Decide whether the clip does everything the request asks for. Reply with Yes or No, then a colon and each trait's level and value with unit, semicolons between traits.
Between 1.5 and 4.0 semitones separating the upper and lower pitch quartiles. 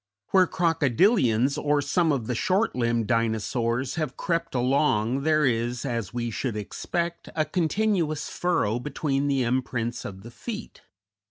No: average, 5.2 semitones